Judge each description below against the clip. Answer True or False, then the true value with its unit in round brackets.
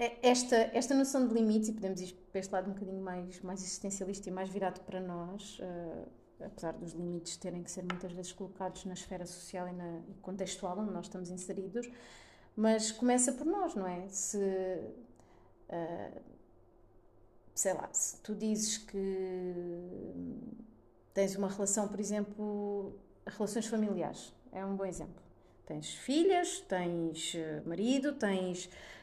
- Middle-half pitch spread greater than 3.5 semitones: False (2.8 semitones)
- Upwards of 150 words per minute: False (145 wpm)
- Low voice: False (190 Hz)